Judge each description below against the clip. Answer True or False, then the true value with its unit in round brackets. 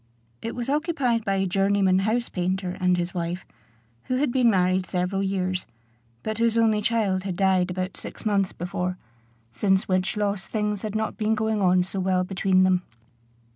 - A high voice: True (195 Hz)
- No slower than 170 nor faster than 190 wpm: True (175 wpm)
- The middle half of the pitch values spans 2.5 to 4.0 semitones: True (2.8 semitones)